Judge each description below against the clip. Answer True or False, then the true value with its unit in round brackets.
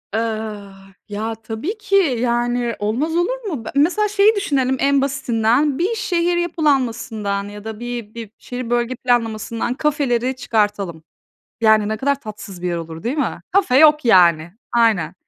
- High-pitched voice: True (240 Hz)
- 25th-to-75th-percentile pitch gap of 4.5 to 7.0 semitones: True (5.1 semitones)